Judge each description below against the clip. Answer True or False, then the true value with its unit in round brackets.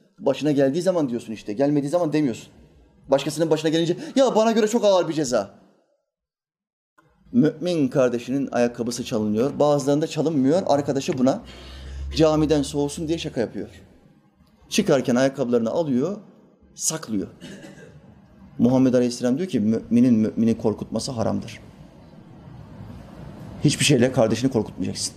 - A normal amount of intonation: False (6.0 semitones)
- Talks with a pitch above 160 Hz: False (145 Hz)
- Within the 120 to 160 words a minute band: False (110 wpm)